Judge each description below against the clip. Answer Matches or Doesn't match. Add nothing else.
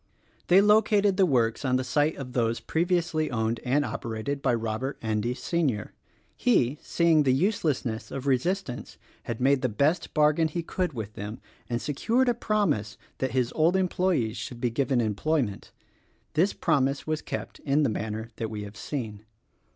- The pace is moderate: Matches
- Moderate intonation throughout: Doesn't match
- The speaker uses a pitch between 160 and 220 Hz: Doesn't match